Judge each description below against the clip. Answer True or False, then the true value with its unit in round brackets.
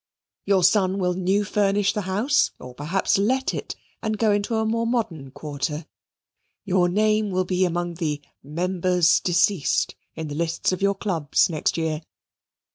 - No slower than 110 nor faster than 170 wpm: True (160 wpm)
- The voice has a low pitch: False (185 Hz)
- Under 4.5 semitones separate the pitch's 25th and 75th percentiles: True (3.9 semitones)